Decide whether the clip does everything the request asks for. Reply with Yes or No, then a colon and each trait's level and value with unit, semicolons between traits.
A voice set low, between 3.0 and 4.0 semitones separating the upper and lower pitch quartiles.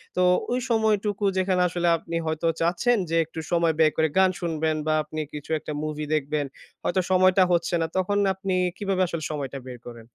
No: medium, 170 Hz; average, 3.4 semitones